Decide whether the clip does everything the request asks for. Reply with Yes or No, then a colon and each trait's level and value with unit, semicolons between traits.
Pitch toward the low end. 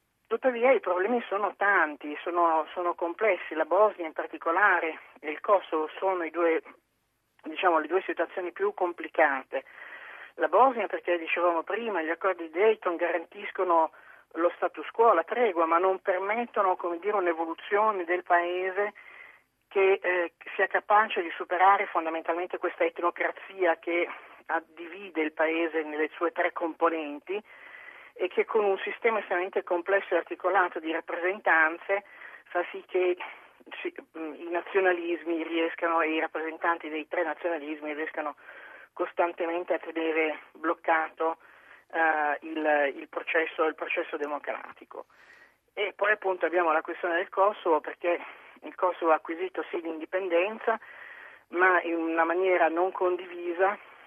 No: medium, 175 Hz